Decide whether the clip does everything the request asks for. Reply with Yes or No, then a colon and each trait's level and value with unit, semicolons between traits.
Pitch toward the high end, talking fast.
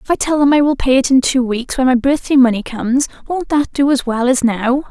Yes: very high, 265 Hz; fast, 280 wpm